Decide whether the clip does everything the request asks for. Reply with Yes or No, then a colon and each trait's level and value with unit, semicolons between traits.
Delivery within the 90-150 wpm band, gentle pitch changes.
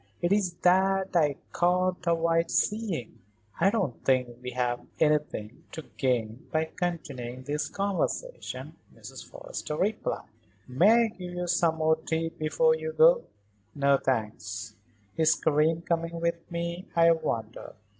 No: slow, 135 wpm; average, 4.7 semitones